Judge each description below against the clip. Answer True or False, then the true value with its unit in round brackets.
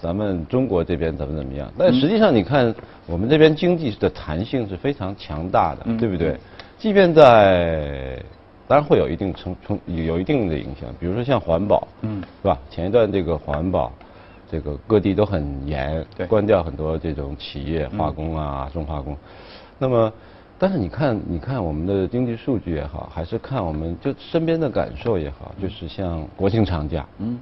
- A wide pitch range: True (5.8 semitones)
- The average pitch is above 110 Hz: False (90 Hz)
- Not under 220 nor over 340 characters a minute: True (280 characters per minute)